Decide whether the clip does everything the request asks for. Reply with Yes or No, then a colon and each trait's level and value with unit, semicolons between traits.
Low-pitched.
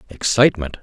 Yes: low, 105 Hz